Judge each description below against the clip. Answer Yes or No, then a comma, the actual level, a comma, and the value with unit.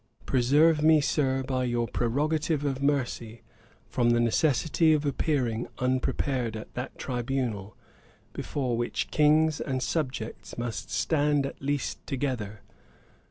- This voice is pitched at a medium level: No, low, 130 Hz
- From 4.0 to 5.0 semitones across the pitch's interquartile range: No, average, 3.6 semitones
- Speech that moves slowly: Yes, slow, 120 wpm